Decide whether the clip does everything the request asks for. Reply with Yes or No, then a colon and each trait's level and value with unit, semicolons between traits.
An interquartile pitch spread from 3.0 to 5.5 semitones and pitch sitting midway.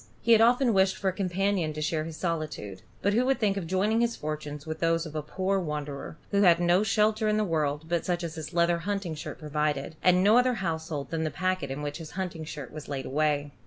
Yes: average, 4.2 semitones; medium, 170 Hz